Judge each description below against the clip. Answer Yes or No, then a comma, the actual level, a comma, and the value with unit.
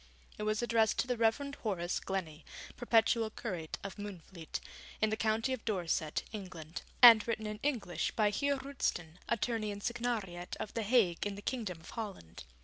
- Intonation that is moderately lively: Yes, average, 4.1 semitones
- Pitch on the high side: Yes, high, 215 Hz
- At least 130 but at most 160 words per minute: No, average, 170 wpm